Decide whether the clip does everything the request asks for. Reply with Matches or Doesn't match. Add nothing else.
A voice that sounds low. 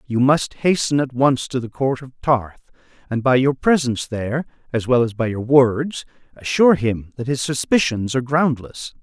Matches